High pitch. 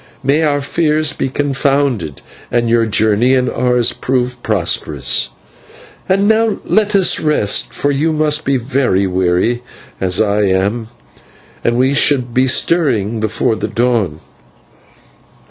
No: low, 125 Hz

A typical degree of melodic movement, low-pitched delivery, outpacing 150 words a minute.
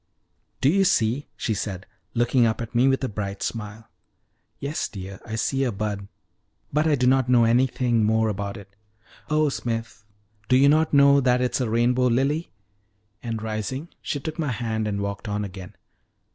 Yes: average, 3.9 semitones; low, 120 Hz; average, 185 wpm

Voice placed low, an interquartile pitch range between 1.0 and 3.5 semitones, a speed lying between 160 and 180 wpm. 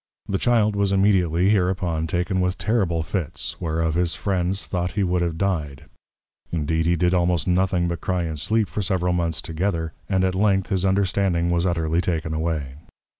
Yes: very low, 90 Hz; narrow, 2.6 semitones; average, 175 wpm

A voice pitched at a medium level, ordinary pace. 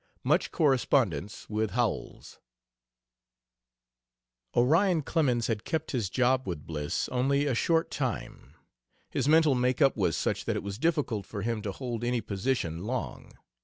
No: low, 125 Hz; average, 145 wpm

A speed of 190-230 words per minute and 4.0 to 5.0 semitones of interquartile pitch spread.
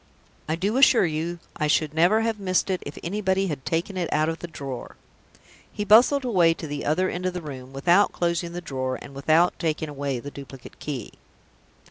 Yes: average, 200 wpm; average, 4.4 semitones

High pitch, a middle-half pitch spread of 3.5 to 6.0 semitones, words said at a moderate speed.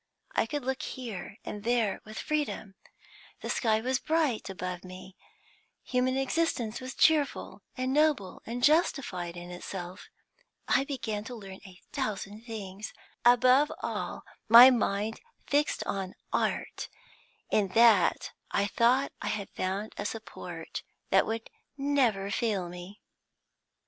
No: high, 225 Hz; average, 4.9 semitones; slow, 130 wpm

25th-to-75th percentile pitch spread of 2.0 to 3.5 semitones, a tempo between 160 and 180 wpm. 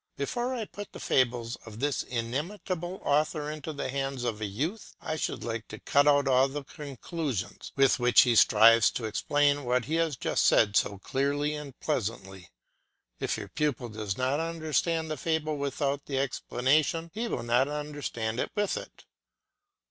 No: average, 4.2 semitones; average, 170 wpm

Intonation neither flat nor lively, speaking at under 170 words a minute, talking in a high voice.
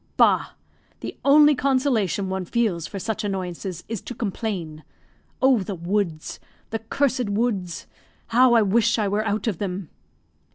Yes: average, 4.0 semitones; average, 150 wpm; high, 210 Hz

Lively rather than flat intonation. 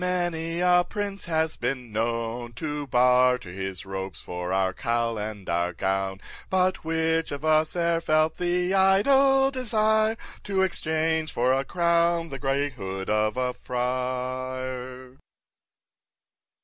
Yes: wide, 6.5 semitones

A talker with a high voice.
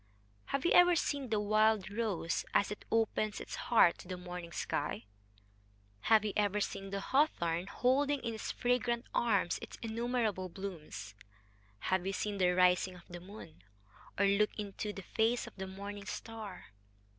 Yes: high, 205 Hz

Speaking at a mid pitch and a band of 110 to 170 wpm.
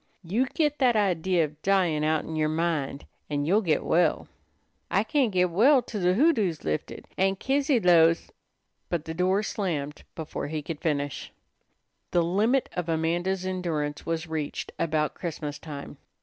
Yes: medium, 170 Hz; average, 165 wpm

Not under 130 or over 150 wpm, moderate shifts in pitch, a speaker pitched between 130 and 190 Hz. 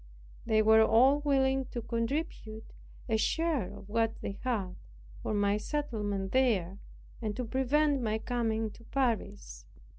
No: average, 140 wpm; average, 3.9 semitones; high, 225 Hz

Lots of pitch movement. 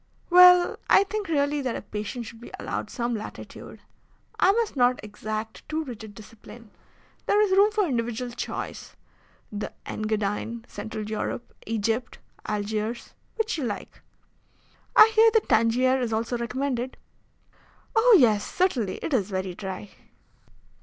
Yes: wide, 5.9 semitones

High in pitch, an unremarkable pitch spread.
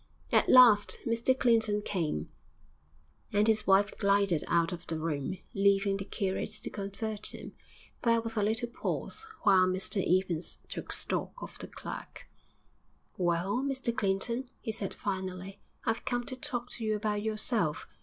Yes: high, 205 Hz; average, 3.4 semitones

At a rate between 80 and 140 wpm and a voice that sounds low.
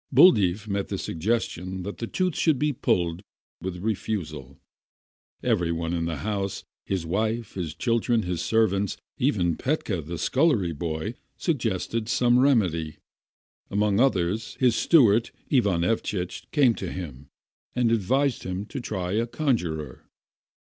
Yes: slow, 135 wpm; low, 100 Hz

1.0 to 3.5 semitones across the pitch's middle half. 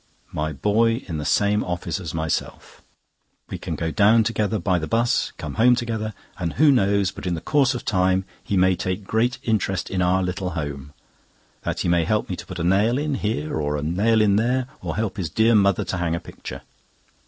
No: average, 4.3 semitones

